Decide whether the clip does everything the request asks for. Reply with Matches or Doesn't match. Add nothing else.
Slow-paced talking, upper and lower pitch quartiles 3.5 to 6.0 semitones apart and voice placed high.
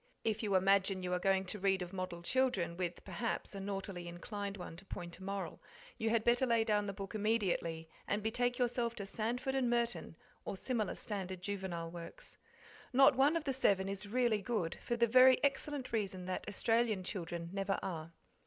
Doesn't match